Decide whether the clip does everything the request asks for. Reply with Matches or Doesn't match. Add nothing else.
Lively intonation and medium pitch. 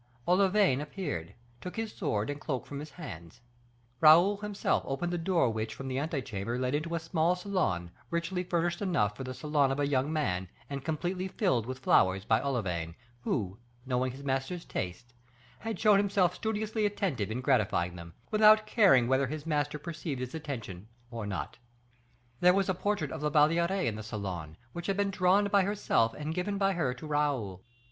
Matches